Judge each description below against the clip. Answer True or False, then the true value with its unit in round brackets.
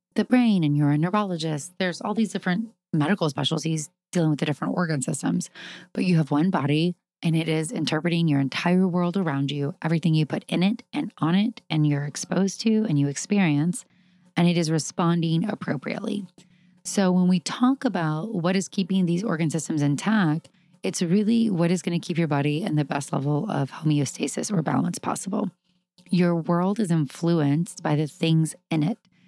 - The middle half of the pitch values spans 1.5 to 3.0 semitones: False (3.4 semitones)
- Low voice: False (175 Hz)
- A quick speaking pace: False (185 wpm)